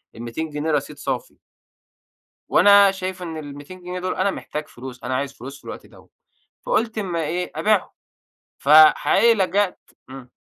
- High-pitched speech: No, medium, 165 Hz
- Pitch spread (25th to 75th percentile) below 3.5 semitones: No, average, 4.9 semitones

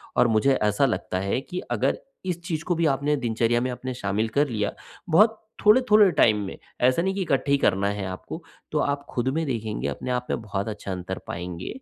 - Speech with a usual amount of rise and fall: No, wide, 6.8 semitones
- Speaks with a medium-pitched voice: No, low, 125 Hz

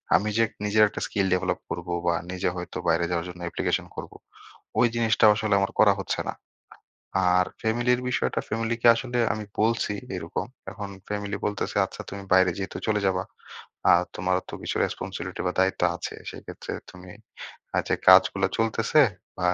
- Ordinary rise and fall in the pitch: Yes, average, 3.4 semitones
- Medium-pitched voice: No, low, 100 Hz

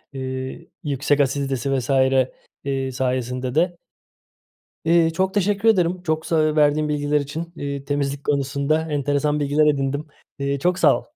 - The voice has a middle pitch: Yes, medium, 145 Hz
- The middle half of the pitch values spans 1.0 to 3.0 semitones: Yes, narrow, 2.6 semitones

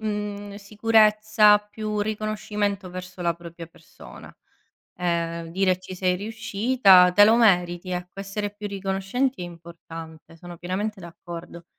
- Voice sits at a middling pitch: No, high, 195 Hz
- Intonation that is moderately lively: Yes, average, 3.1 semitones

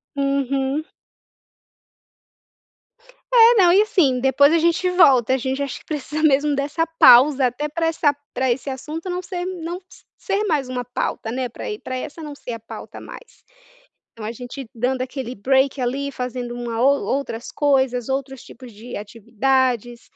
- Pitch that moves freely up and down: No, average, 3.4 semitones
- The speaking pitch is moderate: No, very high, 270 Hz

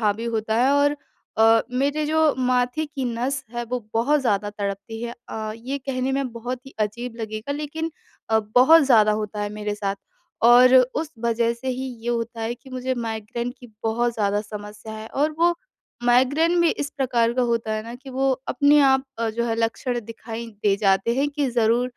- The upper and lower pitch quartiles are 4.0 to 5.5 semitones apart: No, average, 3.2 semitones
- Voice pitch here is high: Yes, high, 240 Hz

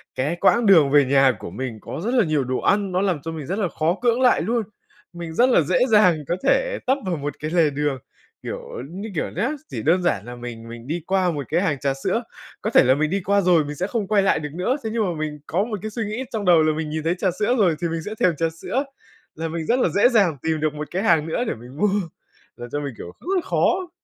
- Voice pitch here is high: No, medium, 170 Hz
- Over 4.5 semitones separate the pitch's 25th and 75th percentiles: Yes, wide, 5.6 semitones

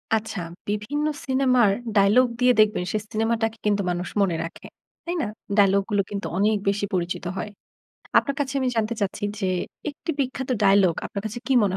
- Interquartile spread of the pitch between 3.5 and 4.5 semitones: Yes, average, 4.0 semitones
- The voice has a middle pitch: No, high, 210 Hz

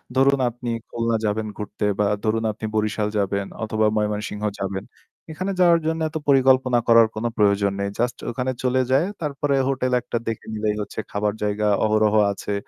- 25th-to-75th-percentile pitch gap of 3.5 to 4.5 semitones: Yes, average, 3.8 semitones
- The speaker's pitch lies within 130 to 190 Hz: No, low, 110 Hz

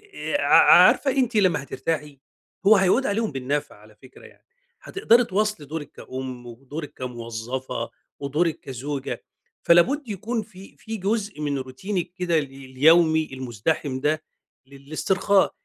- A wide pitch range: Yes, wide, 6.8 semitones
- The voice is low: No, medium, 150 Hz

